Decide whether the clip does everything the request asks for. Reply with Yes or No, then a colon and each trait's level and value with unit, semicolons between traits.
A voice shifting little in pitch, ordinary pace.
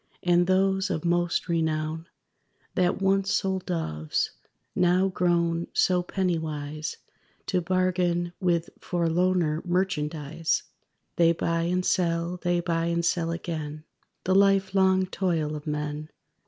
No: narrow, 2.2 semitones; slow, 120 wpm